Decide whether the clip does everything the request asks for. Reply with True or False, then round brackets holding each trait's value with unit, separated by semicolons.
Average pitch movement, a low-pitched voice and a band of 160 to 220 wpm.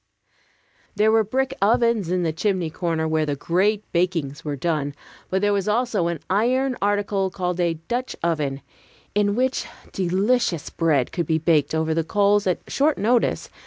False (4.6 semitones; 185 Hz; 165 wpm)